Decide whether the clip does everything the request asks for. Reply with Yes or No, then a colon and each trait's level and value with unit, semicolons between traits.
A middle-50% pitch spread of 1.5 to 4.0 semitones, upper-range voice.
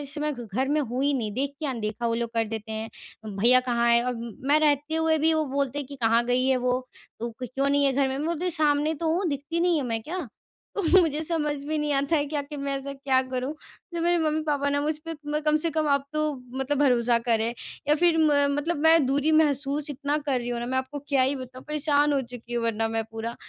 Yes: average, 3.5 semitones; very high, 280 Hz